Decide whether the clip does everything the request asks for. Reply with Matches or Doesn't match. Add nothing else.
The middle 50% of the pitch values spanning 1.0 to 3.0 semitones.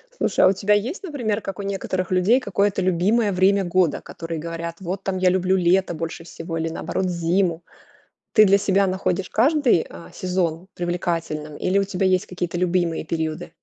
Matches